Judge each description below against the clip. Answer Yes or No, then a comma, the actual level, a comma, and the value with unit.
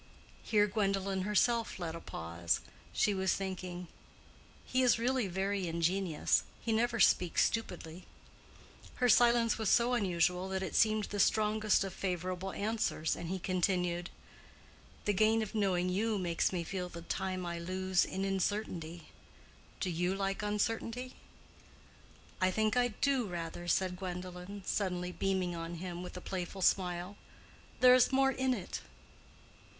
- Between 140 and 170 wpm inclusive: Yes, average, 145 wpm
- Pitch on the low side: No, high, 190 Hz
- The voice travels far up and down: No, average, 3.3 semitones